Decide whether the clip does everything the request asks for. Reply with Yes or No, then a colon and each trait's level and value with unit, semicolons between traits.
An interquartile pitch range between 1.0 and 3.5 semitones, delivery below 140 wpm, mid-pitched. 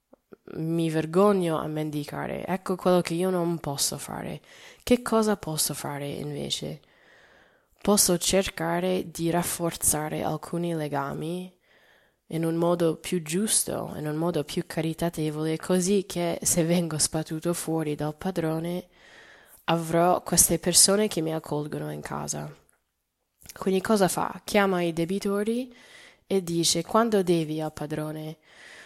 Yes: average, 2.9 semitones; average, 125 wpm; medium, 170 Hz